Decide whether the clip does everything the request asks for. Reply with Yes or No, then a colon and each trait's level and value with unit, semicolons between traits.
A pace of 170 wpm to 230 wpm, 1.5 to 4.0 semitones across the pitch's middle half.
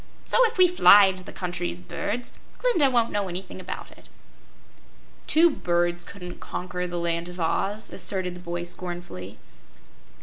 No: average, 160 wpm; average, 3.0 semitones